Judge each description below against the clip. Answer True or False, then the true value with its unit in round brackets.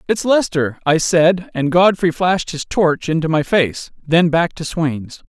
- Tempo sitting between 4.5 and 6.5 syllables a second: False (4.1 syllables/s)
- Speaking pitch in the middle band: True (165 Hz)